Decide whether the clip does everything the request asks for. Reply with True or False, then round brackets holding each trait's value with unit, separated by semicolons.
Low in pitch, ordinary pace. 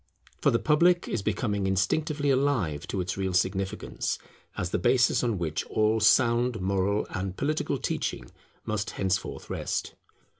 True (105 Hz; 145 wpm)